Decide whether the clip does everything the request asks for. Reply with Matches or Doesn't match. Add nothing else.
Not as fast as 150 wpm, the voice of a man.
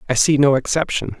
Doesn't match